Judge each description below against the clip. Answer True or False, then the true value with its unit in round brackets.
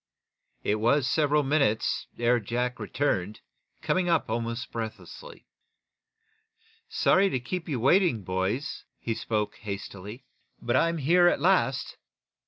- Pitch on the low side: True (125 Hz)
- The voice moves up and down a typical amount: False (5.9 semitones)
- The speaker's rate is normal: False (120 wpm)